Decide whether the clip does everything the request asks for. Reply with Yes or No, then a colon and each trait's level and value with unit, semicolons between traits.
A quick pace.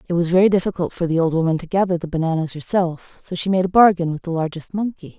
Yes: fast, 255 wpm